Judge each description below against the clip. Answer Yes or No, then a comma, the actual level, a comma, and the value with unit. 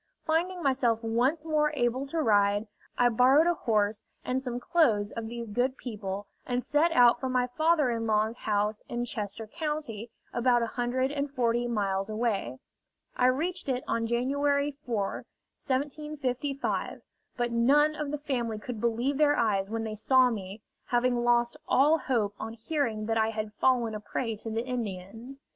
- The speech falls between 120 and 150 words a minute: No, average, 165 wpm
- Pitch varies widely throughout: No, average, 3.7 semitones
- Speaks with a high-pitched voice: Yes, high, 240 Hz